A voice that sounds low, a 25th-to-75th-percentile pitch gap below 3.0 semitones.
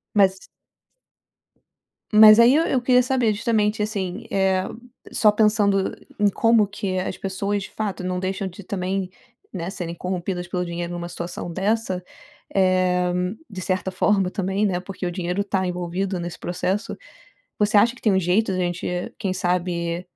No: high, 190 Hz; narrow, 2.5 semitones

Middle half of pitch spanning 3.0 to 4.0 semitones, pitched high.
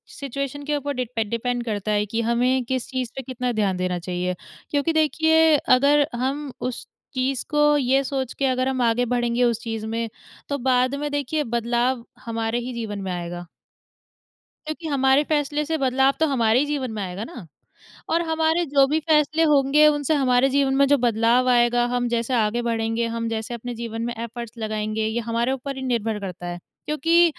Yes: average, 3.6 semitones; very high, 250 Hz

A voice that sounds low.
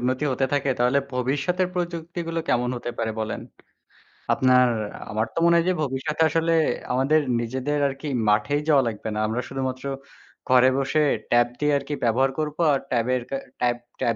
Yes: low, 130 Hz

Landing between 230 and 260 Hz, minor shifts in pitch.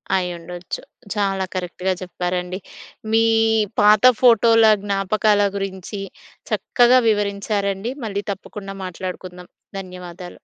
No: high, 195 Hz; narrow, 2.3 semitones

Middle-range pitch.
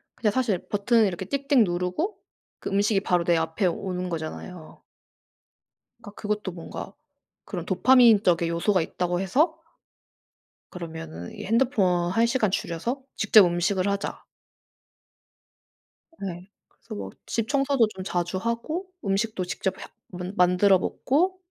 No: high, 195 Hz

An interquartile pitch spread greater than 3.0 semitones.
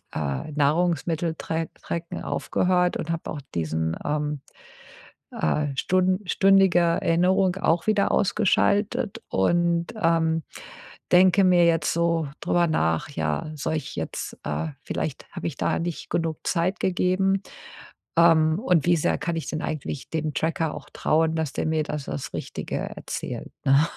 No: average, 2.7 semitones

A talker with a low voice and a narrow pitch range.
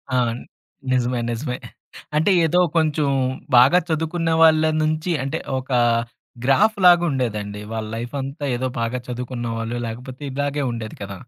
No: low, 130 Hz; average, 4.8 semitones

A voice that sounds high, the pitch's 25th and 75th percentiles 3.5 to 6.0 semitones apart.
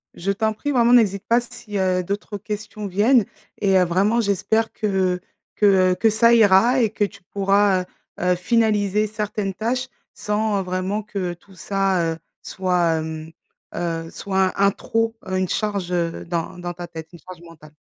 No: high, 195 Hz; average, 2.9 semitones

